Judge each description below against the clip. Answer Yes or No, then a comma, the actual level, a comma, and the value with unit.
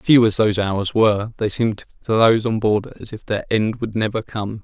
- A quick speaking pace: Yes, fast, 235 wpm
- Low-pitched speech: Yes, low, 110 Hz